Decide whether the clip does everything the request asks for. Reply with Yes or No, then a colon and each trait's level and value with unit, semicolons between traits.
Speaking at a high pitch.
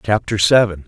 No: low, 105 Hz